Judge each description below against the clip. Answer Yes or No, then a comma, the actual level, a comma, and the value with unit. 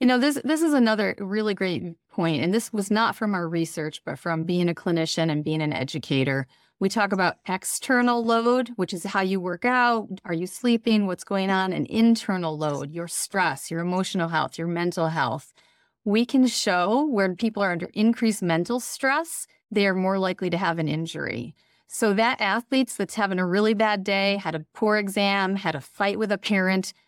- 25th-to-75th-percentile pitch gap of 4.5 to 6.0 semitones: Yes, average, 4.8 semitones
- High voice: Yes, high, 195 Hz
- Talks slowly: No, average, 200 wpm